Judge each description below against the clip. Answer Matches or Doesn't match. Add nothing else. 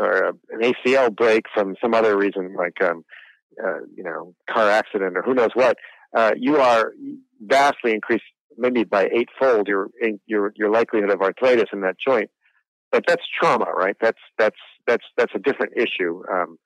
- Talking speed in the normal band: Matches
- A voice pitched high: Doesn't match